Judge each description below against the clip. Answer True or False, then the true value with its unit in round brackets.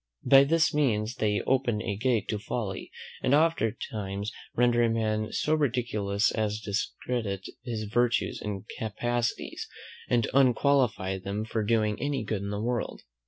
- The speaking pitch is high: False (110 Hz)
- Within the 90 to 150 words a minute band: True (145 wpm)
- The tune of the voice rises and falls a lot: False (2.9 semitones)